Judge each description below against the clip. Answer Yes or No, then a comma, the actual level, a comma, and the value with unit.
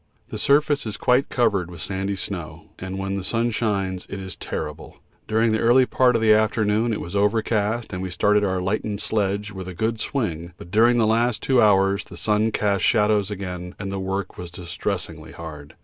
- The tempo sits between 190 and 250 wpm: Yes, average, 200 wpm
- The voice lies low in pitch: Yes, low, 100 Hz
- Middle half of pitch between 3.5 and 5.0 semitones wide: No, average, 2.9 semitones